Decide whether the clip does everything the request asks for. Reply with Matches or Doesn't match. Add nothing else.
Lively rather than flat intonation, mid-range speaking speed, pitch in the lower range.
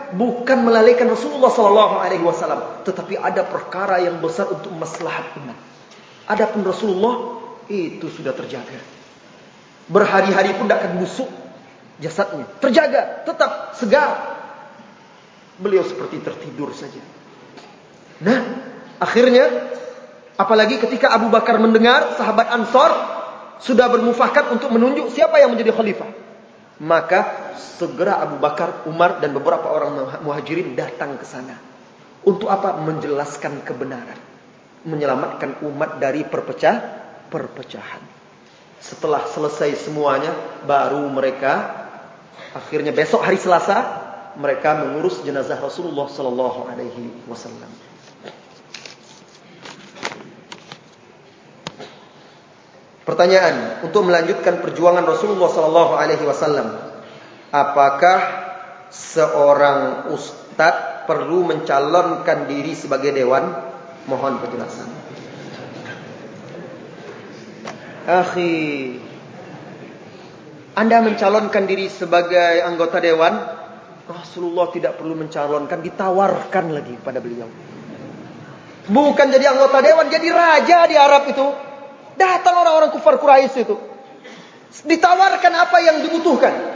Doesn't match